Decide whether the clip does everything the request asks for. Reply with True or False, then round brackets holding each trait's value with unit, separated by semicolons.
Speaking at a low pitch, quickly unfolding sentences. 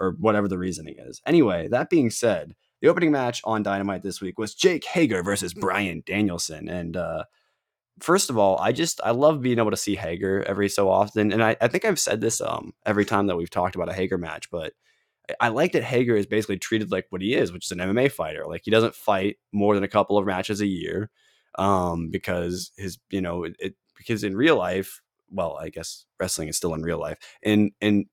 True (100 Hz; 230 wpm)